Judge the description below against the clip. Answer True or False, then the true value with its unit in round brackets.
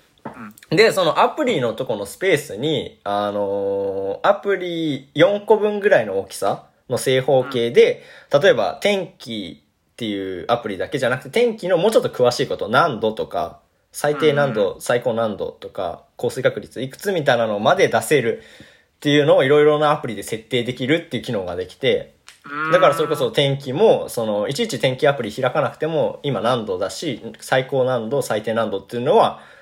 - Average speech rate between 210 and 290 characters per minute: False (355 characters per minute)